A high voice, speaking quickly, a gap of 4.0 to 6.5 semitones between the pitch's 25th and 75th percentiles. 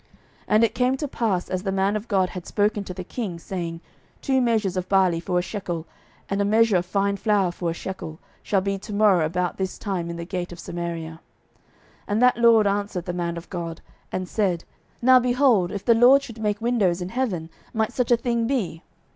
Yes: high, 195 Hz; fast, 220 wpm; average, 4.3 semitones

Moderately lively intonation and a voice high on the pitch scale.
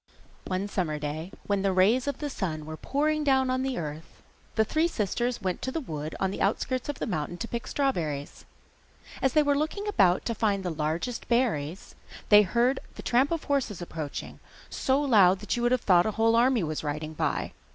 No: wide, 7.2 semitones; high, 210 Hz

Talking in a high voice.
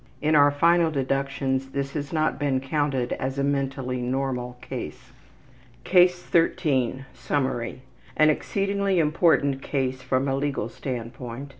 No: low, 135 Hz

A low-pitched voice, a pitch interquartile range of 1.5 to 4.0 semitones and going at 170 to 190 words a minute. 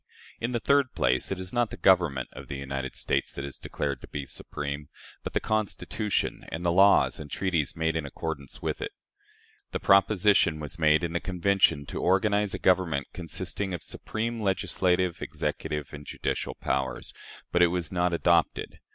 No: very low, 85 Hz; average, 4.7 semitones; average, 175 wpm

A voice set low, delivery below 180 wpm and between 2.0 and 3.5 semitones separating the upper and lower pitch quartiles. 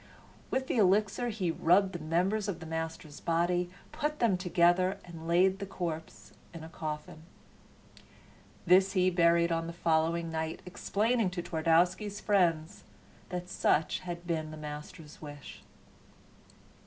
No: medium, 175 Hz; average, 140 wpm; average, 2.8 semitones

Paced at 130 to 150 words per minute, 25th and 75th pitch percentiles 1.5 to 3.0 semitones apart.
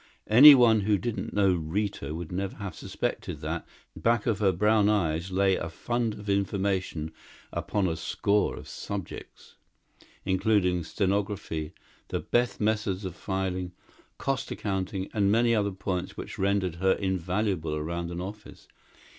Yes: average, 140 wpm; narrow, 2.6 semitones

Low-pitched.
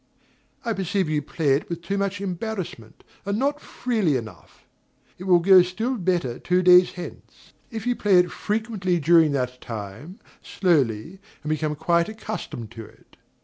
No: medium, 180 Hz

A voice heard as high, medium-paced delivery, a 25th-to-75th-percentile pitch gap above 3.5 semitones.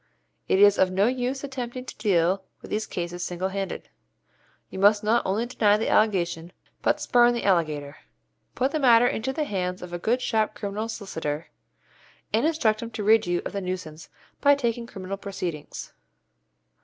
Yes: high, 205 Hz; average, 175 wpm; average, 4.6 semitones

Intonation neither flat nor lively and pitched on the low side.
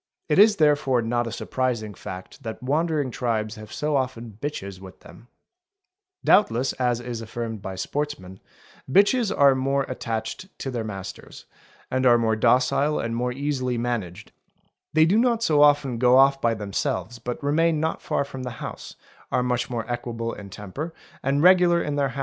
Yes: average, 4.2 semitones; low, 125 Hz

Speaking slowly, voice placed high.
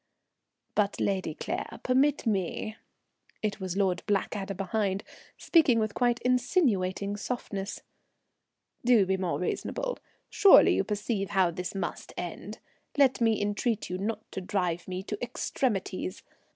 Yes: slow, 130 wpm; high, 205 Hz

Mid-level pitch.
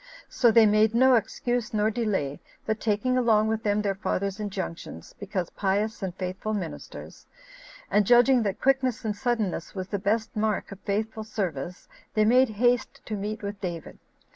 No: high, 215 Hz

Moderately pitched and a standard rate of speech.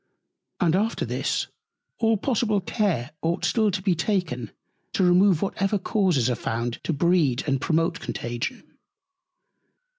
No: medium, 180 Hz; slow, 130 wpm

